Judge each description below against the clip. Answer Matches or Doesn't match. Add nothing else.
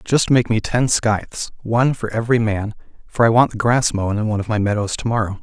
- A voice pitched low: Matches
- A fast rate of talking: Matches